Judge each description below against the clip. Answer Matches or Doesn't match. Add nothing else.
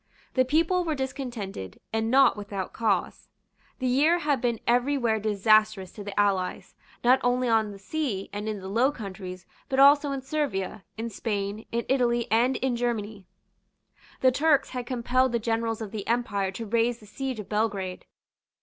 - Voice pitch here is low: Doesn't match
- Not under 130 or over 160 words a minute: Doesn't match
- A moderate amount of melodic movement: Matches